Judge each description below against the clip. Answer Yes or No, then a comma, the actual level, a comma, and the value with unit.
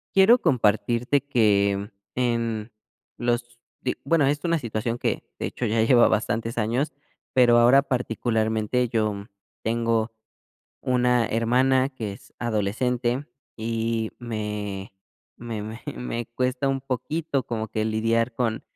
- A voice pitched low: Yes, low, 115 Hz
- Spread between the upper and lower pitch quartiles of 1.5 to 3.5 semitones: Yes, narrow, 2.4 semitones